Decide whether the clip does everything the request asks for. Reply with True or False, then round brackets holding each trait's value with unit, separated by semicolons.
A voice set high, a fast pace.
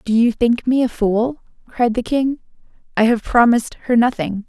False (235 Hz; 190 wpm)